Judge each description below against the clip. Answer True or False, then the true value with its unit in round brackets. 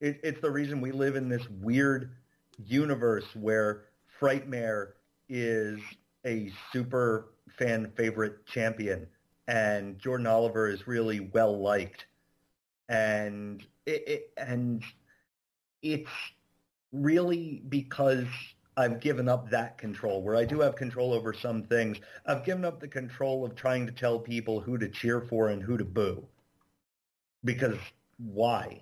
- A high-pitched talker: False (120 Hz)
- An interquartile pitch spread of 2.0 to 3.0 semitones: False (3.7 semitones)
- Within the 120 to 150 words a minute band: True (135 wpm)